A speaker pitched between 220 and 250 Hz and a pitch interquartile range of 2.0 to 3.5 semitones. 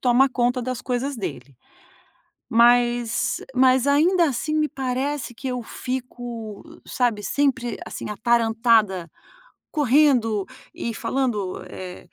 Yes: high, 245 Hz; average, 2.8 semitones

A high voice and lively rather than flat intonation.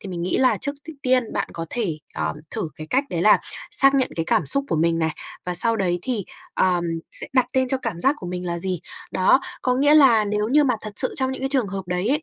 Yes: high, 215 Hz; wide, 6.7 semitones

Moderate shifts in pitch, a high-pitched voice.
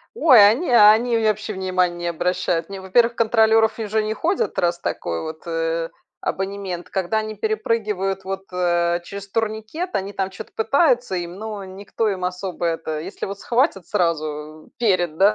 Yes: average, 3.9 semitones; high, 195 Hz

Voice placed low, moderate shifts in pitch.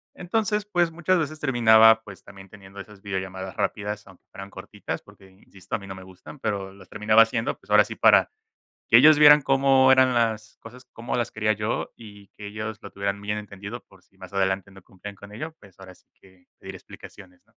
Yes: low, 105 Hz; average, 3.8 semitones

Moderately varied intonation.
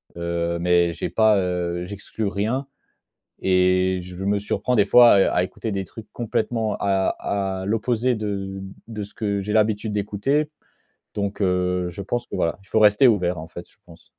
Yes: average, 3.1 semitones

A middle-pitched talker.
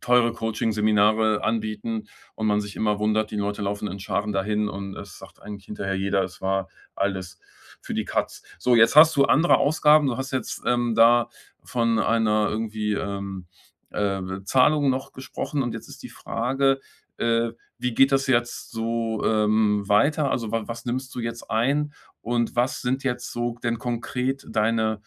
No: low, 115 Hz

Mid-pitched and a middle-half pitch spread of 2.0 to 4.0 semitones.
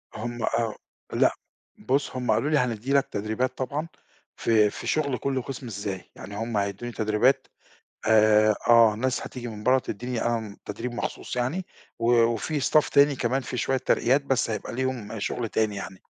No: low, 120 Hz; average, 3.3 semitones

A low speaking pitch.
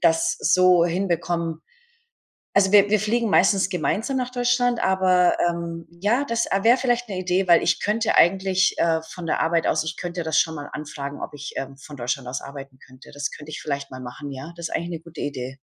No: medium, 170 Hz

